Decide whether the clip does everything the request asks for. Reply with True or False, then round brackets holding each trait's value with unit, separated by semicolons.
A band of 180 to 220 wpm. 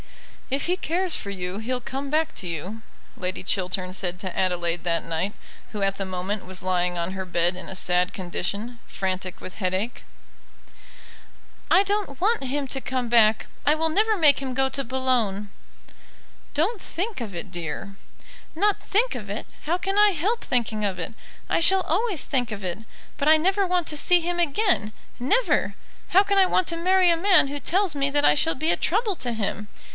True (195 wpm)